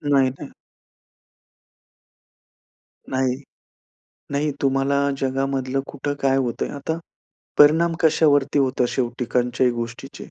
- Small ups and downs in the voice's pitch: Yes, narrow, 1.8 semitones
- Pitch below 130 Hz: No, low, 135 Hz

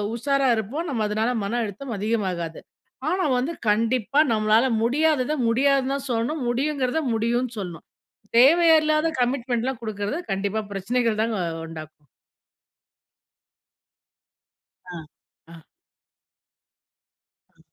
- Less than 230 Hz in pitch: No, high, 240 Hz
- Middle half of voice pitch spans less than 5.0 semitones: Yes, average, 4.5 semitones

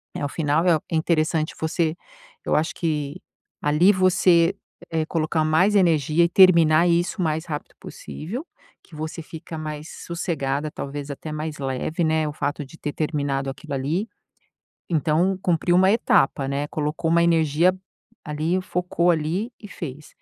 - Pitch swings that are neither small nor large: No, narrow, 2.3 semitones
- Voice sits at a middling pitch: Yes, medium, 160 Hz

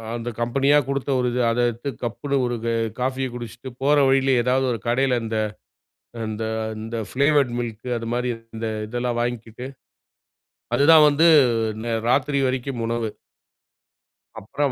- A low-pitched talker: Yes, low, 125 Hz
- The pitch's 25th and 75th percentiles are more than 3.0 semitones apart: No, narrow, 2.6 semitones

